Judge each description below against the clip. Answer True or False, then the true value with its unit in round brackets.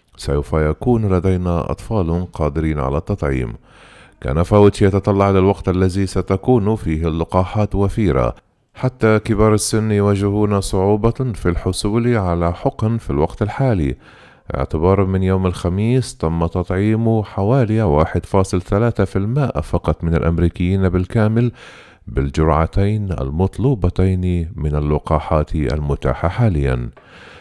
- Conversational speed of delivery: True (100 wpm)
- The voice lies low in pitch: True (95 Hz)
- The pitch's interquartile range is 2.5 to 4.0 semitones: False (4.4 semitones)